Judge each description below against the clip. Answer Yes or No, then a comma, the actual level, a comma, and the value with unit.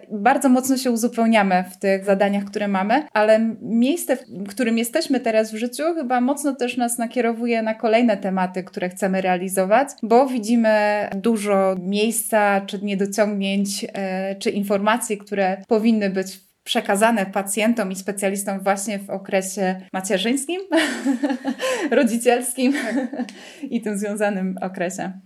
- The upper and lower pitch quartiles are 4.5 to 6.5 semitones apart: No, average, 3.6 semitones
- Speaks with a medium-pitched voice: No, high, 215 Hz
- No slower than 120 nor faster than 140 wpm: Yes, average, 125 wpm